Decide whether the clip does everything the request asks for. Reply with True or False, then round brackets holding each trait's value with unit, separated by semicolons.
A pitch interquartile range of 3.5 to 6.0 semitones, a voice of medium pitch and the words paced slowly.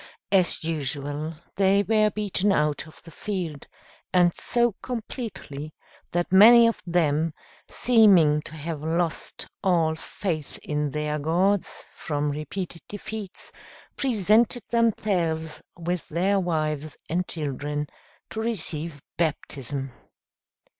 True (4.9 semitones; 170 Hz; 110 wpm)